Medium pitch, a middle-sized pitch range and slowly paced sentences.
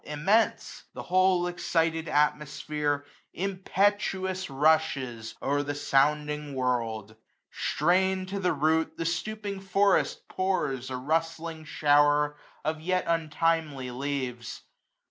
Yes: medium, 155 Hz; average, 4.2 semitones; slow, 105 wpm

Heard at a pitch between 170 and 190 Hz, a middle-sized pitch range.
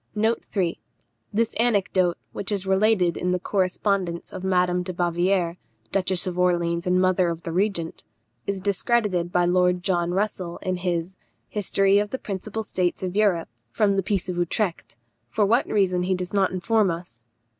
No: medium, 185 Hz; narrow, 2.2 semitones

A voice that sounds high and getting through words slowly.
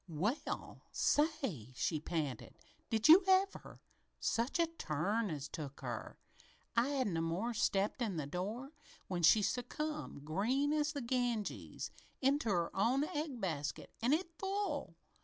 No: high, 230 Hz; average, 145 wpm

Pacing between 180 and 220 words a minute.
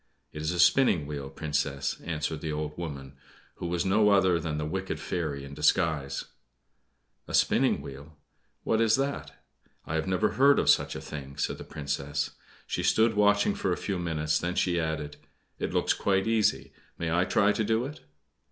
Yes: average, 185 wpm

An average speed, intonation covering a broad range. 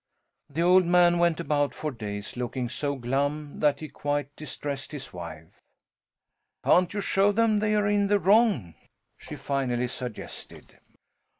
Yes: average, 145 wpm; wide, 5.8 semitones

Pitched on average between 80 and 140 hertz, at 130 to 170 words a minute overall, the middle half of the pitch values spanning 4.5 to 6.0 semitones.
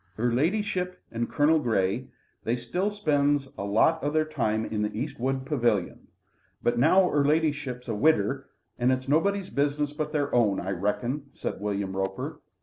Yes: low, 135 Hz; average, 165 wpm; average, 5.1 semitones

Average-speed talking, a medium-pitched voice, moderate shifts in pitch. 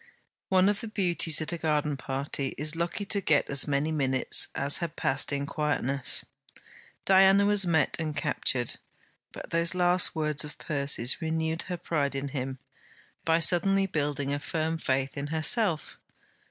Yes: average, 160 wpm; medium, 155 Hz; average, 3.5 semitones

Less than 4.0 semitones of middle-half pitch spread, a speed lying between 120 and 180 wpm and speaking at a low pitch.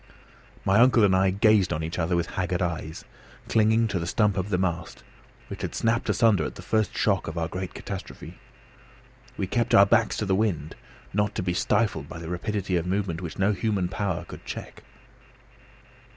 No: average, 3.4 semitones; average, 195 wpm; very low, 95 Hz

